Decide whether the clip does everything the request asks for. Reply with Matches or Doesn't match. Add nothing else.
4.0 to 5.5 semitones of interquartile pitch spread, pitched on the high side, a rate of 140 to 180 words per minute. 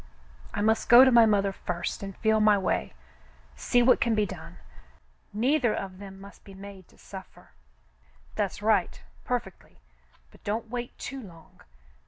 Matches